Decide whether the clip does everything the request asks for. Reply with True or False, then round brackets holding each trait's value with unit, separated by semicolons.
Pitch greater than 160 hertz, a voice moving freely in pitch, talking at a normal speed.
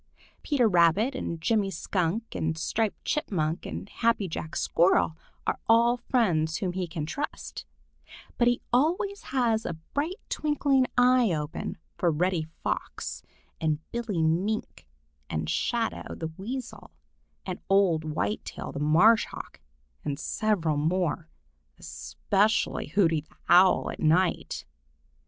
False (190 Hz; 6.4 semitones; 125 wpm)